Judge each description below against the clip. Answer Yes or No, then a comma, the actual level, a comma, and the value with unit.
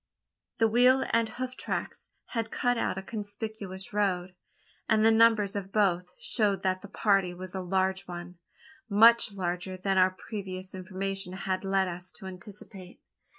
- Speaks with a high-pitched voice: Yes, high, 195 Hz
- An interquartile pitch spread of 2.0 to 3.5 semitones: Yes, narrow, 2.5 semitones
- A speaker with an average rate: Yes, average, 155 wpm